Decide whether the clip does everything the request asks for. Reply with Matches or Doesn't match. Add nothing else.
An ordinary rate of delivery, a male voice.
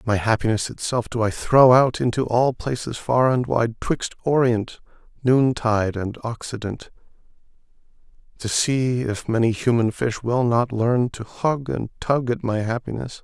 Matches